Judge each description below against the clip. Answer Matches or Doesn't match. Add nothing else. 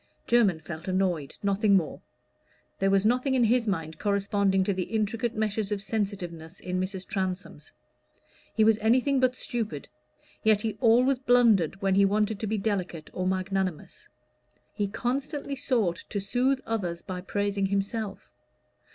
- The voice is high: Matches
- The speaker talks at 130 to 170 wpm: Matches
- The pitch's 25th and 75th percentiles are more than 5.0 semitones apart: Doesn't match